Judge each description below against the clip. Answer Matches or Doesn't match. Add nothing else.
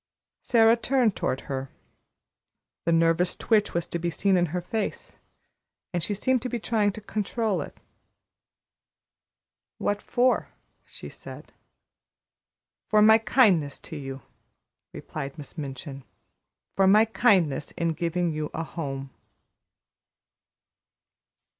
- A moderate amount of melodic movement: Doesn't match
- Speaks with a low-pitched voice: Doesn't match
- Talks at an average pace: Doesn't match